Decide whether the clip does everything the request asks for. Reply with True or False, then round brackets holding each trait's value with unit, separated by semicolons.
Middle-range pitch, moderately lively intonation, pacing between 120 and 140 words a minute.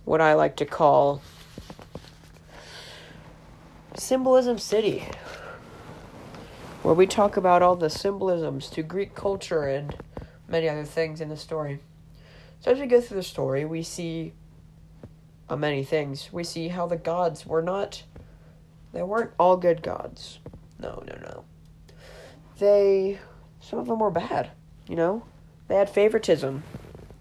True (165 Hz; 4.3 semitones; 135 wpm)